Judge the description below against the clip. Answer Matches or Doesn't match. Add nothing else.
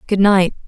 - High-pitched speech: Matches